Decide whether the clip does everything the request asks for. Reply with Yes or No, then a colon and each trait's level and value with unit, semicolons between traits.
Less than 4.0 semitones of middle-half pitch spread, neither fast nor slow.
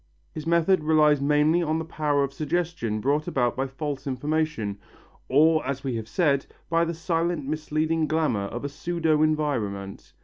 Yes: average, 2.9 semitones; average, 165 wpm